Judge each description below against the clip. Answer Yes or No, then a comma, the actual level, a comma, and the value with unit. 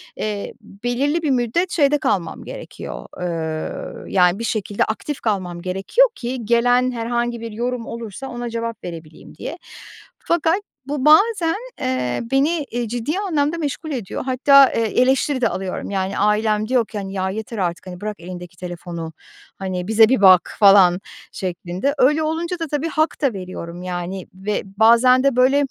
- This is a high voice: Yes, high, 230 Hz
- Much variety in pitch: Yes, wide, 6.4 semitones